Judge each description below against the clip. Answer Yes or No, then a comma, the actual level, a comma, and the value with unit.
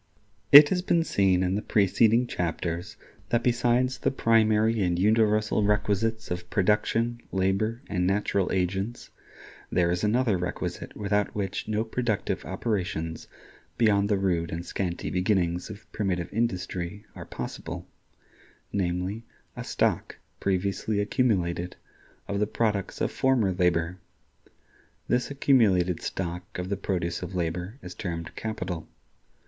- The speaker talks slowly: Yes, slow, 125 wpm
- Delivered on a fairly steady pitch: No, average, 3.6 semitones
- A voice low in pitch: Yes, low, 100 Hz